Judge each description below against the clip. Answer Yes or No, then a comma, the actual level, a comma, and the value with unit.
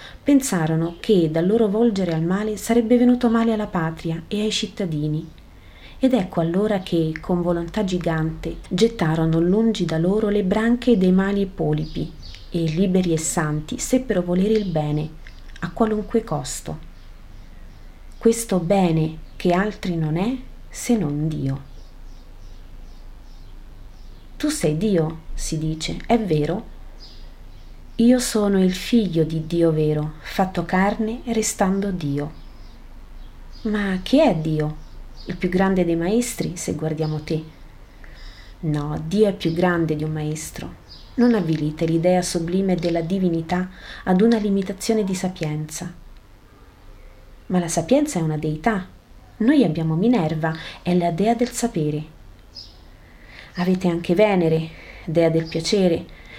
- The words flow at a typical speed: Yes, average, 130 wpm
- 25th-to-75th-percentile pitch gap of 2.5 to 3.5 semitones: No, average, 4.8 semitones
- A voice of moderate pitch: Yes, medium, 175 Hz